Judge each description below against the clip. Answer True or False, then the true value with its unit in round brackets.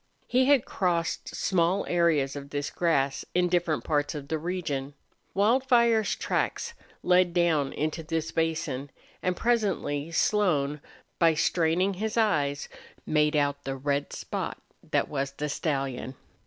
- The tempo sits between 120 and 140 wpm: True (135 wpm)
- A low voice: False (160 Hz)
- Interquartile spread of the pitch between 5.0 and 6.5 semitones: False (4.3 semitones)